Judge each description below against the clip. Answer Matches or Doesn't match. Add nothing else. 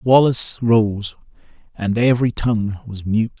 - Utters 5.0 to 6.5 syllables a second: Doesn't match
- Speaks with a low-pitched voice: Matches